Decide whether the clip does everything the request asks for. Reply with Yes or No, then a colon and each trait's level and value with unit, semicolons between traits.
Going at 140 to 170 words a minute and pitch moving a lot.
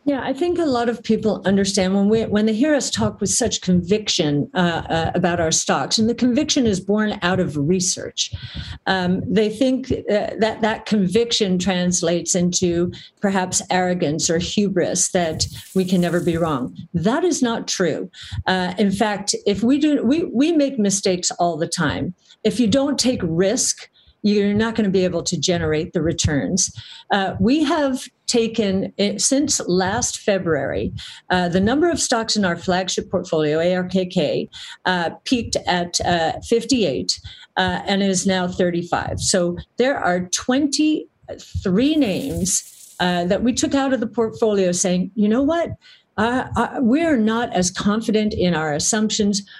No: average, 165 wpm; average, 4.6 semitones